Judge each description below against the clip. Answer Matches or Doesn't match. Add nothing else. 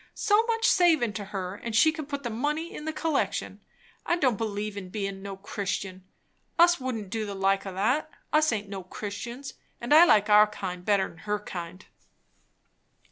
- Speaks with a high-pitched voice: Matches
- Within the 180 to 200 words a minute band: Matches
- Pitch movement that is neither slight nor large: Doesn't match